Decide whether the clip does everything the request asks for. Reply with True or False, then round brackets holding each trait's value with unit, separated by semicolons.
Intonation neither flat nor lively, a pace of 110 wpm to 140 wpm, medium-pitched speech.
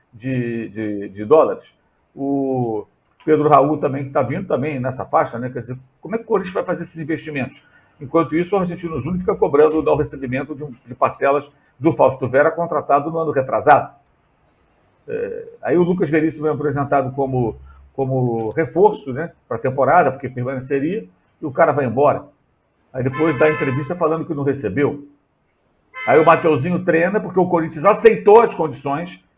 False (4.0 semitones; 170 wpm; 145 Hz)